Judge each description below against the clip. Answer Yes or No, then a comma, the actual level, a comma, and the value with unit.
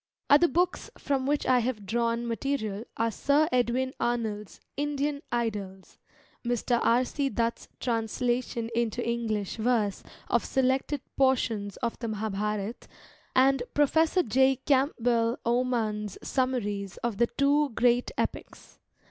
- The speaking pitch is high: Yes, high, 240 Hz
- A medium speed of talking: No, slow, 125 wpm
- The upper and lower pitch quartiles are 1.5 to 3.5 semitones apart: Yes, average, 3.1 semitones